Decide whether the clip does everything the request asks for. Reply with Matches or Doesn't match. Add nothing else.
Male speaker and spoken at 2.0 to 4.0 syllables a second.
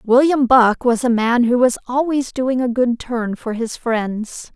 Doesn't match